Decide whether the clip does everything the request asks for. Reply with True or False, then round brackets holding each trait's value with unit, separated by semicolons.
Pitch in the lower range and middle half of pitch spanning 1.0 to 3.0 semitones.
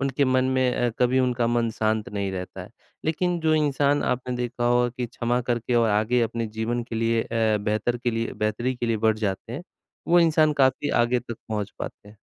True (120 Hz; 2.5 semitones)